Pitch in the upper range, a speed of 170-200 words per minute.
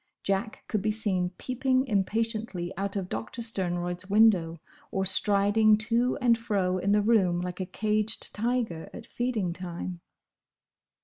No: high, 205 Hz; average, 140 wpm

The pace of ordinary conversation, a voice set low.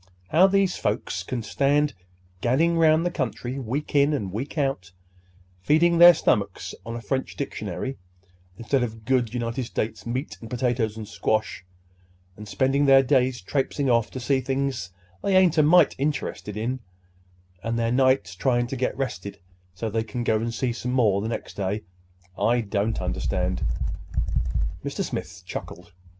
Yes: average, 160 wpm; low, 125 Hz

